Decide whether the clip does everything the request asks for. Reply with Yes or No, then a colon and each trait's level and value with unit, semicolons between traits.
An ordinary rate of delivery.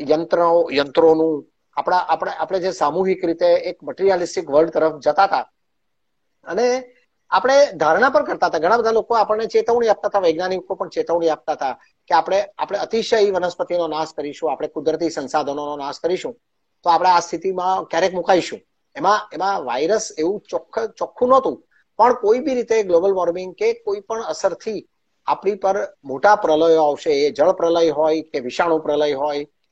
No: fast, 160 wpm